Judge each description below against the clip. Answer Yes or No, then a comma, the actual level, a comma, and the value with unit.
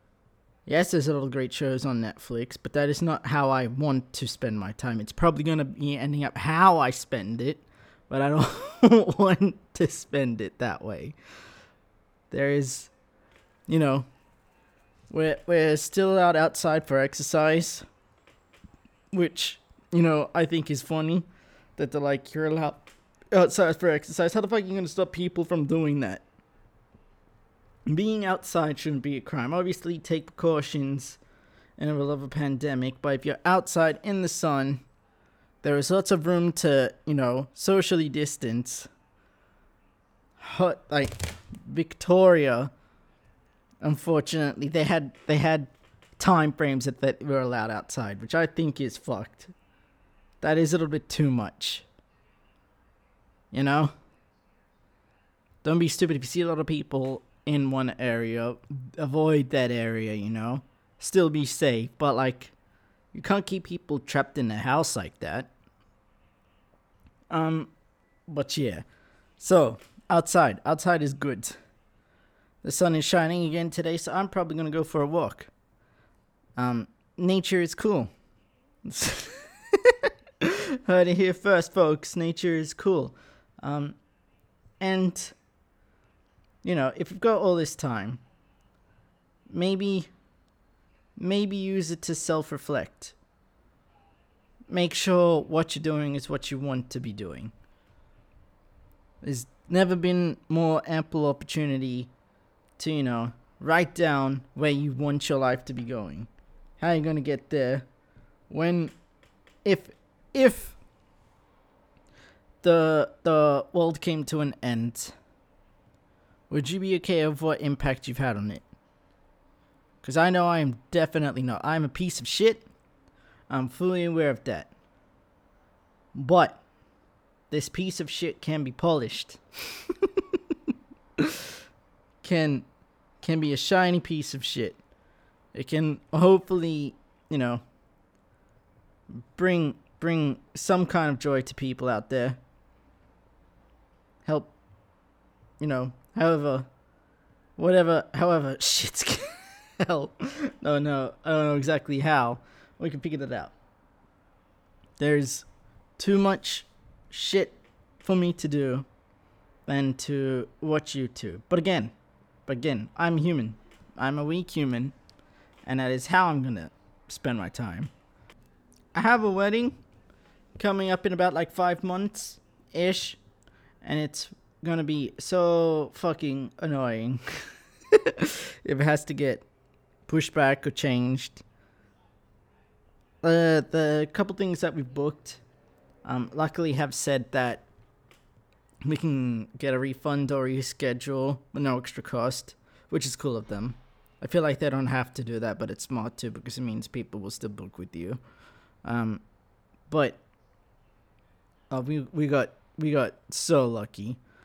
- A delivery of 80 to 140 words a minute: Yes, slow, 135 wpm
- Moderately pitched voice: Yes, medium, 145 Hz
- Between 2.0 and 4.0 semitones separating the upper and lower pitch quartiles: No, average, 5.2 semitones